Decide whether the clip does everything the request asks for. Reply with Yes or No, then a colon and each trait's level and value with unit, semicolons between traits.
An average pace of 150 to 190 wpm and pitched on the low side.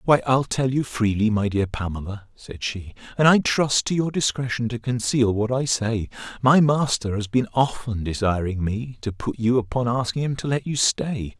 No: average, 200 wpm; low, 120 Hz